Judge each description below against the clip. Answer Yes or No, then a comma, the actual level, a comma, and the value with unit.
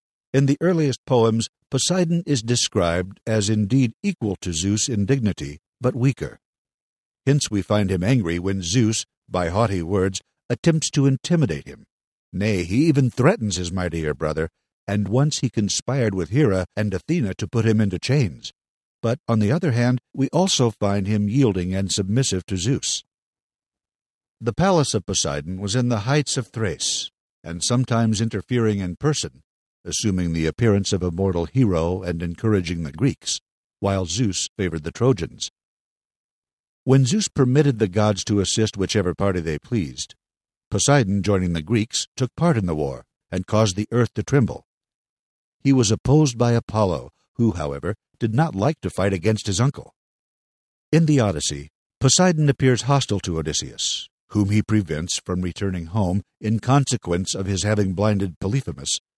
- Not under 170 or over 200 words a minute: No, average, 160 wpm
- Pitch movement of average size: No, wide, 5.8 semitones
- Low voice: Yes, low, 110 Hz